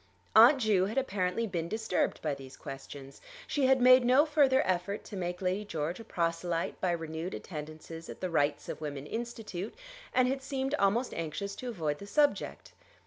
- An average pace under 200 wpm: Yes, average, 180 wpm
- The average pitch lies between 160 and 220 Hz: Yes, high, 190 Hz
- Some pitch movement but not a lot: No, wide, 6.7 semitones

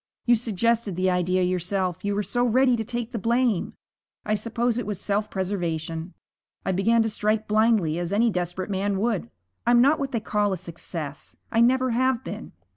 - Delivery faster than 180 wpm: Yes, average, 190 wpm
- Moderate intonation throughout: Yes, average, 4.2 semitones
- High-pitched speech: Yes, high, 210 Hz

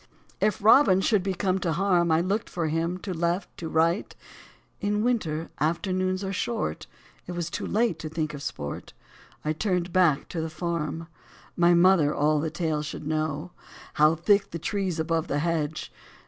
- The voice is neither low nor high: Yes, medium, 170 Hz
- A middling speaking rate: Yes, average, 180 wpm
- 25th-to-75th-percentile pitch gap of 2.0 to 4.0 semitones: Yes, average, 3.0 semitones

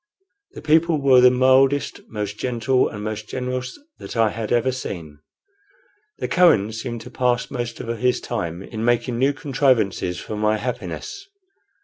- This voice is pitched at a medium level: No, low, 120 Hz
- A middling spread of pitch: Yes, average, 3.3 semitones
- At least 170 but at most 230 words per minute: No, average, 155 wpm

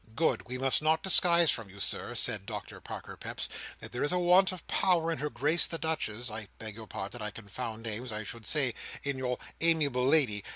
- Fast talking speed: Yes, fast, 210 wpm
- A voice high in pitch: No, low, 130 Hz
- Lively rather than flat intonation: Yes, wide, 6.4 semitones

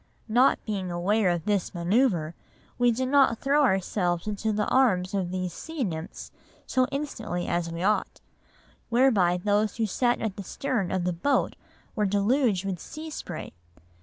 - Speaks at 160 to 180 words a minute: Yes, average, 165 wpm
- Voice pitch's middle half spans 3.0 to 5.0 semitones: No, wide, 5.5 semitones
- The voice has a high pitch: Yes, high, 205 Hz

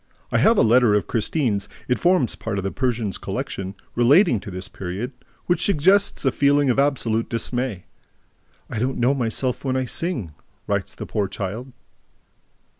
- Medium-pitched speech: No, low, 120 Hz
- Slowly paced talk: No, average, 165 wpm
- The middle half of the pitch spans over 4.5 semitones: Yes, average, 5.0 semitones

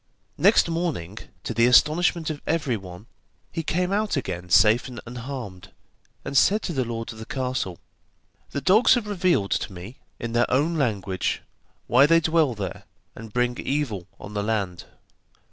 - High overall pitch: No, low, 125 Hz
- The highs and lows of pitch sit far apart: Yes, wide, 7.4 semitones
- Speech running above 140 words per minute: Yes, average, 160 wpm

